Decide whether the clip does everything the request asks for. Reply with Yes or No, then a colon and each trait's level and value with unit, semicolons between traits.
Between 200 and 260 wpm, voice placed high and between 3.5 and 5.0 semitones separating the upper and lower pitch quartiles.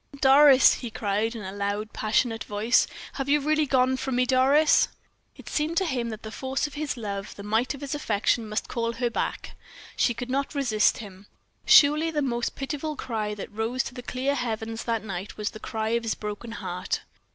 Yes: fast, 205 wpm; high, 235 Hz; average, 4.0 semitones